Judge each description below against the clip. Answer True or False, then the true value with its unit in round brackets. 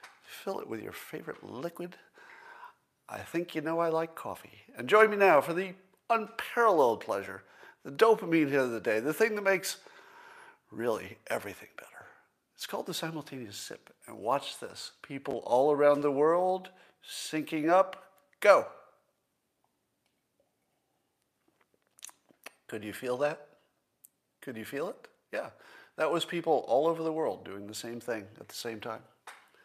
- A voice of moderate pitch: True (170 Hz)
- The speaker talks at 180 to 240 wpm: False (150 wpm)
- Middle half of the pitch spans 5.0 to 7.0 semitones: True (5.4 semitones)